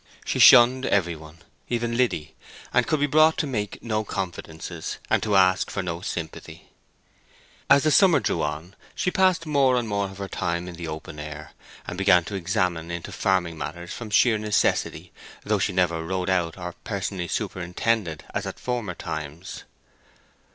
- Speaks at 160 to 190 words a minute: Yes, average, 165 wpm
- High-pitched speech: No, very low, 95 Hz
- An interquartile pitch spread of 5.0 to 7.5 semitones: Yes, wide, 5.4 semitones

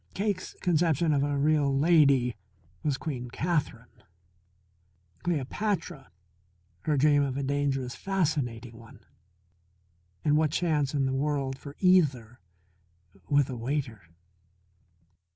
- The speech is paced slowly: Yes, slow, 110 wpm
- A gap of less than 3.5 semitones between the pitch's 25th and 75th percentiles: Yes, average, 2.9 semitones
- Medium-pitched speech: Yes, medium, 145 Hz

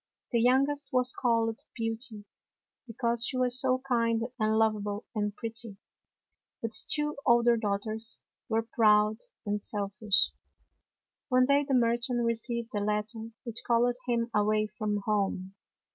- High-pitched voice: Yes, high, 230 Hz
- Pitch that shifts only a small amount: Yes, narrow, 2.3 semitones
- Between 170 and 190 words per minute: No, slow, 135 wpm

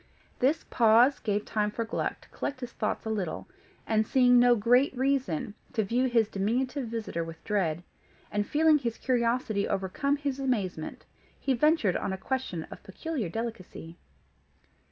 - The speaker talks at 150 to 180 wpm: Yes, average, 155 wpm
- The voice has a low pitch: No, high, 230 Hz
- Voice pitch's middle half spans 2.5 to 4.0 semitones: No, average, 4.4 semitones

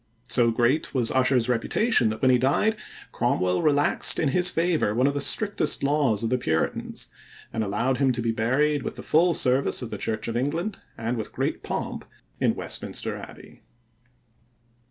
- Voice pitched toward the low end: Yes, low, 130 Hz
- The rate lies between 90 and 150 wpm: No, average, 175 wpm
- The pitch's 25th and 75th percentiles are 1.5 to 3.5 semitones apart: No, average, 4.4 semitones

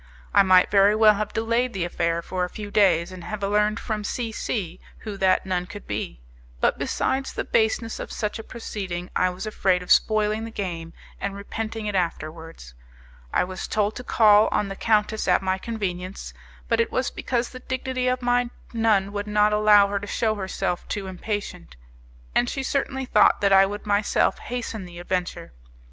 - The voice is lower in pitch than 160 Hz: No, high, 205 Hz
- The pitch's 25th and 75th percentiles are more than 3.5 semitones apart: No, average, 3.0 semitones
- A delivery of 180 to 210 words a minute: Yes, average, 190 wpm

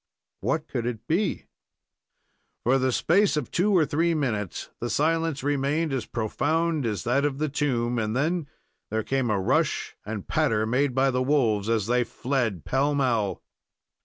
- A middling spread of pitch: Yes, average, 4.6 semitones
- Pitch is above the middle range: No, low, 130 Hz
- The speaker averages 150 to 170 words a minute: Yes, average, 165 wpm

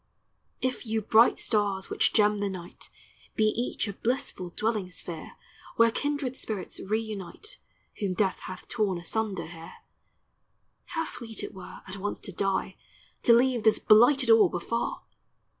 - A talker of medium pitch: No, high, 215 Hz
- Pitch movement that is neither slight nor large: Yes, average, 3.4 semitones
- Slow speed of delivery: No, average, 145 wpm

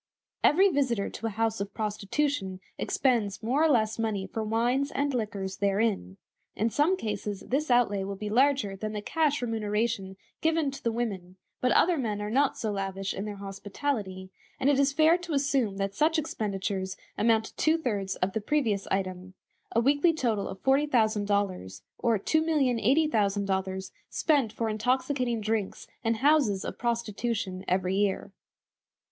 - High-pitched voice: Yes, high, 220 Hz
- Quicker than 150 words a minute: Yes, average, 160 wpm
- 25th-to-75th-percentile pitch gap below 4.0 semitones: No, wide, 5.4 semitones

